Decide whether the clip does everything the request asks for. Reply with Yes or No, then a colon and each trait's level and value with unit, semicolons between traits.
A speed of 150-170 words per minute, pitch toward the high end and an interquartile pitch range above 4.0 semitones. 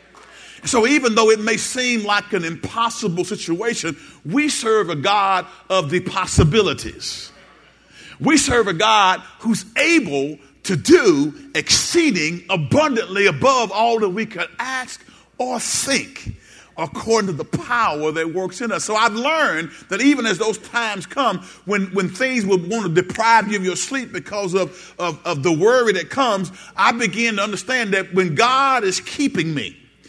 Yes: average, 160 wpm; high, 210 Hz; average, 4.6 semitones